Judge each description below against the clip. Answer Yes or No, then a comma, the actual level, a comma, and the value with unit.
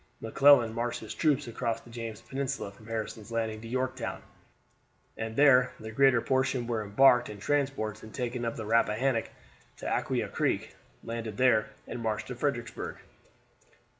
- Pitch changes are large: No, average, 2.7 semitones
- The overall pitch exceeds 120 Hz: No, low, 115 Hz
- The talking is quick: No, average, 155 wpm